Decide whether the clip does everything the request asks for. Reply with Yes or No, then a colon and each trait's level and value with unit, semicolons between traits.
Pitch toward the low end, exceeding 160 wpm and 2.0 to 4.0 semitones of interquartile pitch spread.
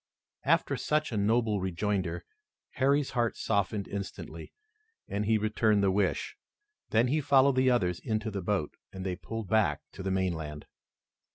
No: low, 105 Hz; average, 155 wpm; average, 3.7 semitones